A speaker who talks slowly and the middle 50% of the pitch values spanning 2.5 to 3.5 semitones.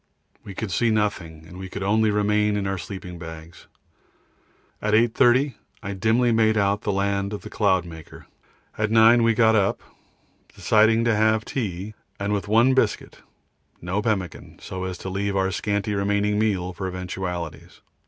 No: average, 165 wpm; average, 2.8 semitones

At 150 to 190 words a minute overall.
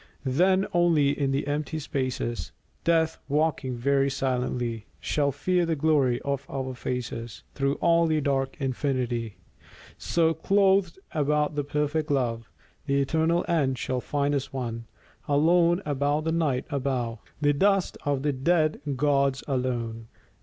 No: average, 140 wpm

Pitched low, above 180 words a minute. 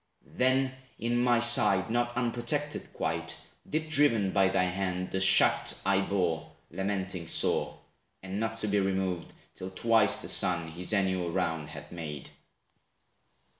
No: very low, 95 Hz; average, 140 wpm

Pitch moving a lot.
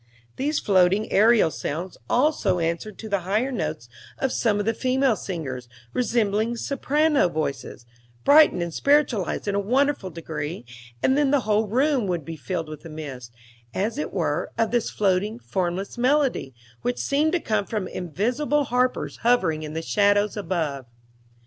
Yes: wide, 7.0 semitones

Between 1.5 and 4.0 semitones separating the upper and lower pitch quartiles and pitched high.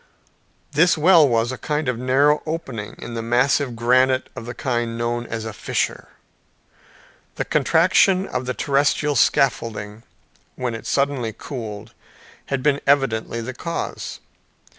No: average, 3.6 semitones; low, 130 Hz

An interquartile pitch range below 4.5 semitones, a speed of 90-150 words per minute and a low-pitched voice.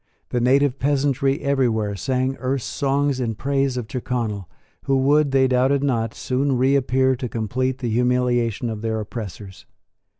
Yes: average, 2.7 semitones; average, 145 wpm; low, 130 Hz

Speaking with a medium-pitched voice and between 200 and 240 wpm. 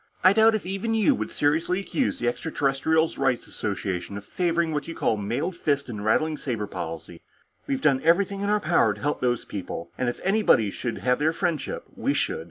Yes: medium, 145 Hz; fast, 205 wpm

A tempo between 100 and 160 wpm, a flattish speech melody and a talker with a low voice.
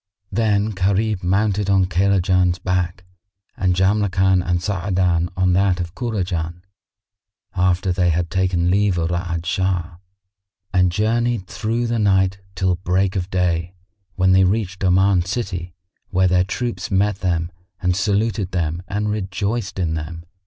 Yes: average, 140 wpm; narrow, 2.0 semitones; very low, 95 Hz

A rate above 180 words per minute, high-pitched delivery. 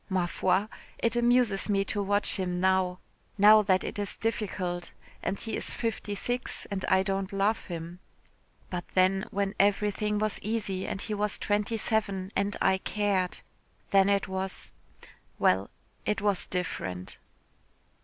No: average, 150 wpm; high, 195 Hz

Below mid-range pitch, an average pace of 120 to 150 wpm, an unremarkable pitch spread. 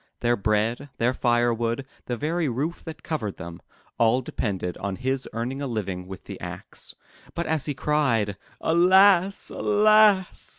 No: low, 125 Hz; average, 145 wpm; wide, 6.3 semitones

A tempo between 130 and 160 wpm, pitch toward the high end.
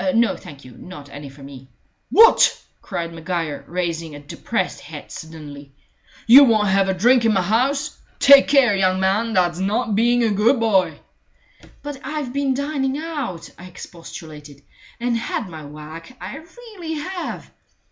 Yes: average, 155 wpm; high, 200 Hz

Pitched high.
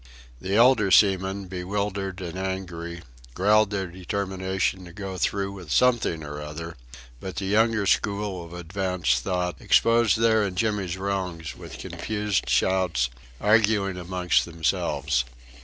No: very low, 95 Hz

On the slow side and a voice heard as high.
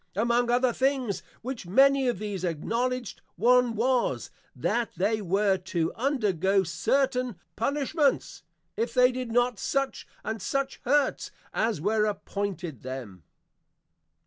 Yes: slow, 120 wpm; high, 230 Hz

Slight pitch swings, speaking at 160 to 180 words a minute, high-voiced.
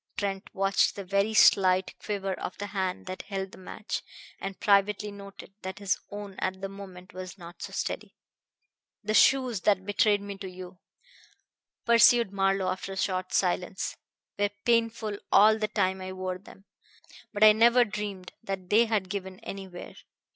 Yes: narrow, 1.9 semitones; average, 165 wpm; high, 195 Hz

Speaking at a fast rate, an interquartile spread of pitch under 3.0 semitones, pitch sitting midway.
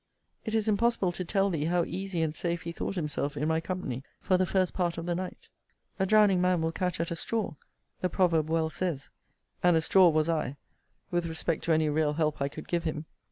Yes: fast, 225 wpm; narrow, 2.6 semitones; medium, 170 Hz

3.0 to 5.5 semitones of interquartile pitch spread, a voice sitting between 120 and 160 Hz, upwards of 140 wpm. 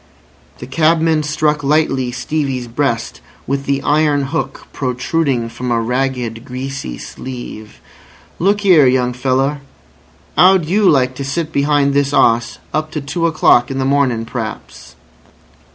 No: average, 3.4 semitones; low, 135 Hz; slow, 135 wpm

